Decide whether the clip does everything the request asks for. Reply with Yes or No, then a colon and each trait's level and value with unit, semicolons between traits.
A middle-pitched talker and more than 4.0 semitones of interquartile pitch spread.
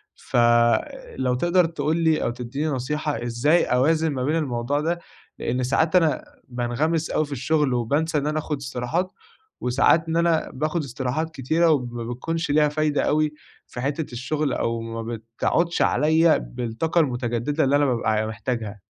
Yes: medium, 145 Hz; average, 4.6 semitones